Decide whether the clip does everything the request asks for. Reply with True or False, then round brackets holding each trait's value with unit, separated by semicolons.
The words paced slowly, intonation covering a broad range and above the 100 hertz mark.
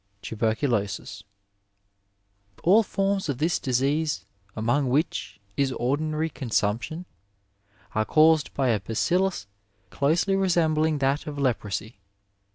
True (105 wpm; 6.5 semitones; 140 Hz)